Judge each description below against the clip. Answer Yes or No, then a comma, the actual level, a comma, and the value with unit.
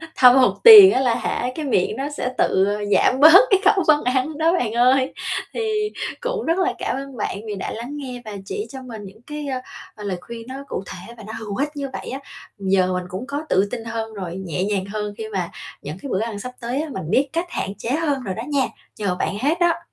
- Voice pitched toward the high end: Yes, very high, 250 Hz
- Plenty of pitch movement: Yes, wide, 6.1 semitones